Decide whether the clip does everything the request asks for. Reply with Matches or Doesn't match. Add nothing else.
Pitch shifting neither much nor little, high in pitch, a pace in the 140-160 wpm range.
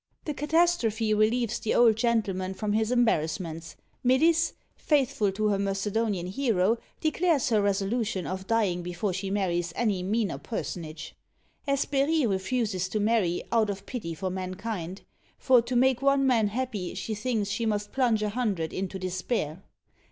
Matches